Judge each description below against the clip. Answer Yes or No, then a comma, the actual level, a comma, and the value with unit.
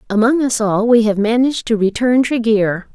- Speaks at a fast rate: No, average, 185 wpm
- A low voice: No, high, 230 Hz